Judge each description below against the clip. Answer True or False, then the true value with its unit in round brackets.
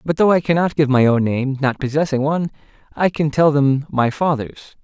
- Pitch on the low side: False (145 Hz)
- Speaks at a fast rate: True (210 wpm)